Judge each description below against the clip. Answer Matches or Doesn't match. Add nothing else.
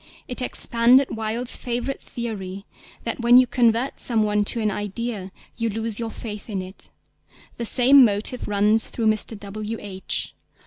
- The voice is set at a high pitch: Matches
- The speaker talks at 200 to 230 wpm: Doesn't match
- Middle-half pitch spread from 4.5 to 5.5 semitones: Doesn't match